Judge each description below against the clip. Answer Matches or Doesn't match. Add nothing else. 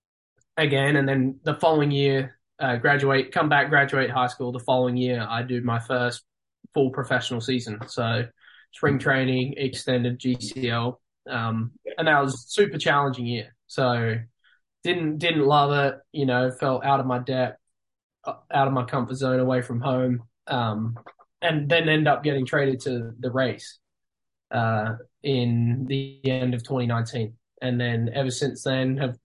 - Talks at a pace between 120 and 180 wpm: Matches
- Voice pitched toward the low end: Matches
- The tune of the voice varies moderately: Doesn't match